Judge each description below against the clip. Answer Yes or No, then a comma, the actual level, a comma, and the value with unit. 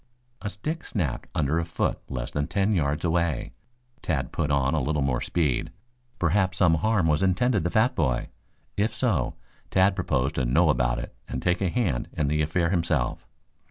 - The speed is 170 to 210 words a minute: Yes, average, 185 wpm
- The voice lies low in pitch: Yes, very low, 85 Hz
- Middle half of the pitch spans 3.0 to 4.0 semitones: No, average, 5.3 semitones